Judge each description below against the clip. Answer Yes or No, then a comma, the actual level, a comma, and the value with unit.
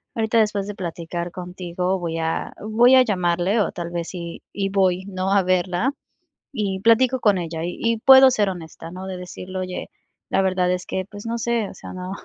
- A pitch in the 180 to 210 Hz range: Yes, high, 190 Hz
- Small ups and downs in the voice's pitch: No, average, 3.2 semitones